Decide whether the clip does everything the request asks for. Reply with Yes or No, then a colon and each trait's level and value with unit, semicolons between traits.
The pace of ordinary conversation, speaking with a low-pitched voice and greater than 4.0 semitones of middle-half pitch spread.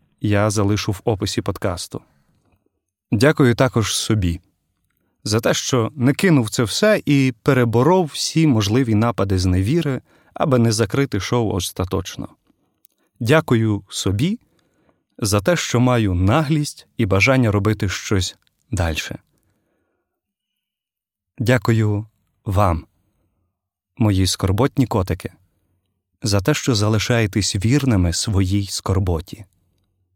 No: slow, 100 wpm; low, 105 Hz; average, 4.8 semitones